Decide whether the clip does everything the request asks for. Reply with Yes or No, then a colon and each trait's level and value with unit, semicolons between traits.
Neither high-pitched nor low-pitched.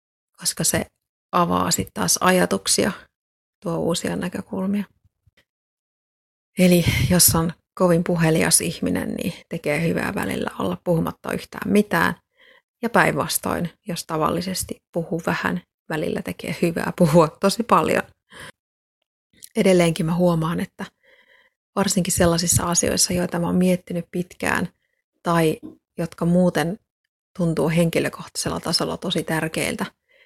Yes: medium, 175 Hz